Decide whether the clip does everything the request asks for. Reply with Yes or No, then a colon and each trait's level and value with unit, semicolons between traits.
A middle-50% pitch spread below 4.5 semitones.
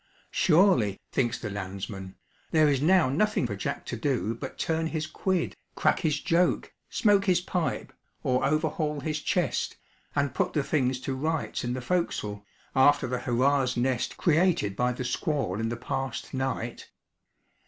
No: average, 4.8 semitones